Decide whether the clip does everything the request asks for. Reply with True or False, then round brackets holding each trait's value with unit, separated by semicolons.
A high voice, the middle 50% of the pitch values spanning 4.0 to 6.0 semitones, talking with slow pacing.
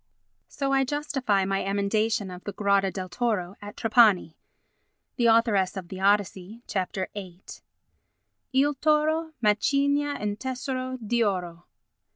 True (210 Hz; 5.1 semitones; 130 wpm)